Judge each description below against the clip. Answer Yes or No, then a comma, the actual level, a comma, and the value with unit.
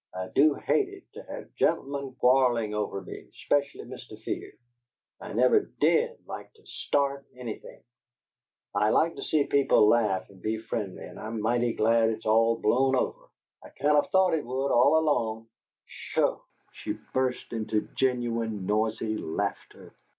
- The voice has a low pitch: Yes, low, 120 Hz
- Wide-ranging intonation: No, average, 4.2 semitones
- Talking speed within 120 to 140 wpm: No, average, 155 wpm